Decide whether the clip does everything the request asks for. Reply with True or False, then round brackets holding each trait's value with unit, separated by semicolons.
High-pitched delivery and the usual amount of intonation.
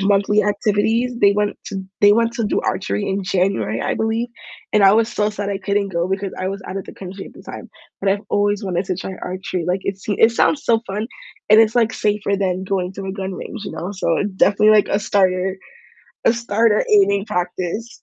False (200 Hz; 1.8 semitones)